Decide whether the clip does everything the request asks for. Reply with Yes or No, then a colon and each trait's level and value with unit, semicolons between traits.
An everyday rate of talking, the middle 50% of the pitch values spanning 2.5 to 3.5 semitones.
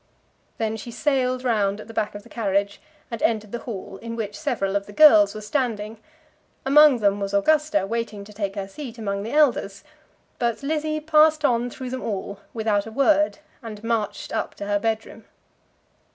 No: average, 190 wpm; average, 4.1 semitones